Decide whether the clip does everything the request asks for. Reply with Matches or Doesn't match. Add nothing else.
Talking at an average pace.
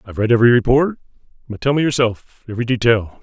Matches